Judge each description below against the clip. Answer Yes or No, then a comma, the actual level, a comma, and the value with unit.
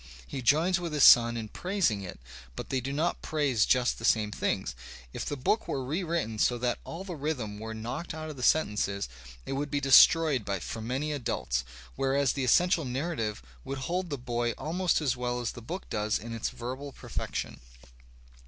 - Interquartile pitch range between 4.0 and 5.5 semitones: Yes, average, 5.1 semitones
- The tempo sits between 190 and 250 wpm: Yes, average, 195 wpm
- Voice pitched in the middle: No, low, 130 Hz